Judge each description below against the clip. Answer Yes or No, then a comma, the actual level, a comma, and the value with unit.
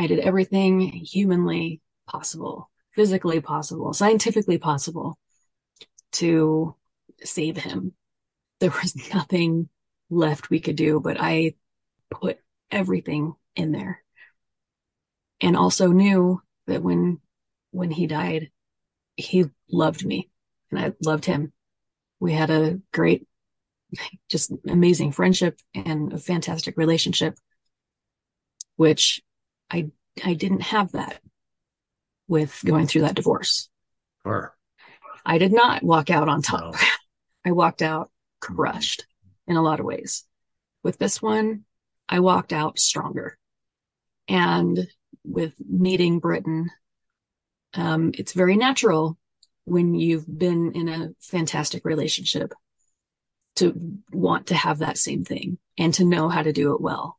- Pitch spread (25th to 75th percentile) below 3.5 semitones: Yes, narrow, 2.6 semitones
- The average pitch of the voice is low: No, medium, 165 Hz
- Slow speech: Yes, slow, 120 wpm